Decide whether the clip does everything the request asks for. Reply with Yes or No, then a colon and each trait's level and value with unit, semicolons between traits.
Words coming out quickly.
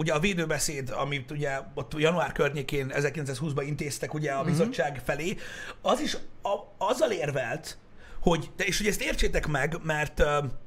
No: average, 145 wpm